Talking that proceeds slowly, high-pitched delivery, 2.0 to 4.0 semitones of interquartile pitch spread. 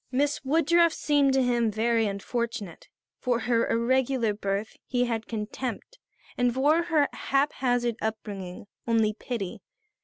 Yes: slow, 125 wpm; high, 240 Hz; average, 3.6 semitones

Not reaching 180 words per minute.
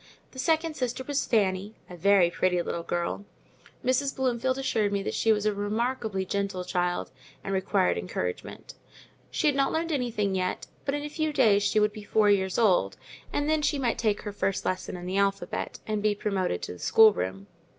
No: average, 190 wpm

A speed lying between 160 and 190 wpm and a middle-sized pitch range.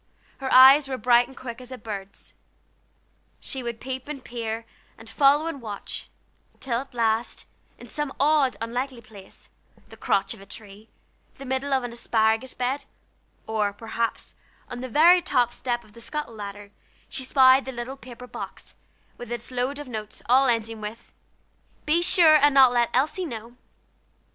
Yes: average, 170 wpm; average, 3.0 semitones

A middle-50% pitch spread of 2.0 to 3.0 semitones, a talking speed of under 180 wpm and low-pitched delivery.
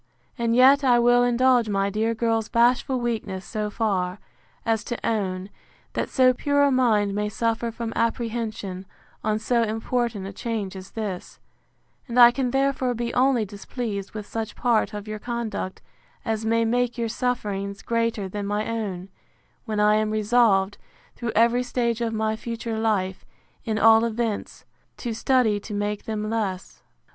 No: narrow, 2.4 semitones; average, 160 wpm; high, 225 Hz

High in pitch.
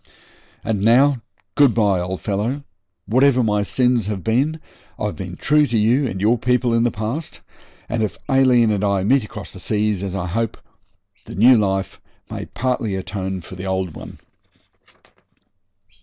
No: low, 110 Hz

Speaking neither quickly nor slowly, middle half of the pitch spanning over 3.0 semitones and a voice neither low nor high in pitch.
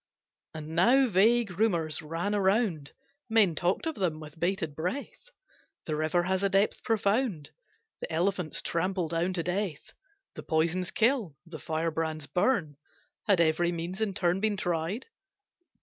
Yes: average, 145 wpm; average, 4.1 semitones; medium, 180 Hz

